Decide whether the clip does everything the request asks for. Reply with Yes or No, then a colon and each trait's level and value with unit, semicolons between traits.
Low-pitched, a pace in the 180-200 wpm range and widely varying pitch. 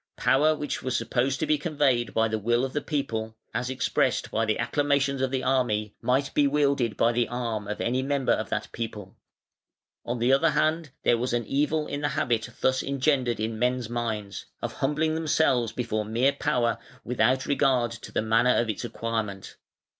No: low, 125 Hz; average, 190 wpm; average, 3.4 semitones